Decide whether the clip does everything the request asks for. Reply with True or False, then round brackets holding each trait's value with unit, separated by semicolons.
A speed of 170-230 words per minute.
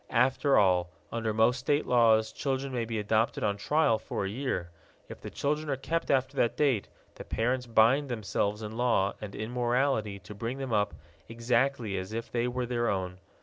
True (190 wpm)